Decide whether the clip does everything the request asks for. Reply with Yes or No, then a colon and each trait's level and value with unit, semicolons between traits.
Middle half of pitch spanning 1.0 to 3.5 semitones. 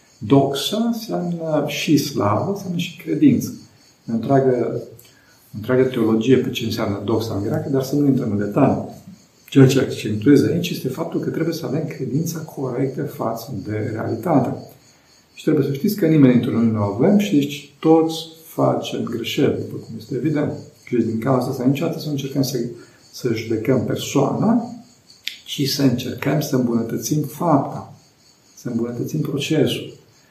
No: average, 4.3 semitones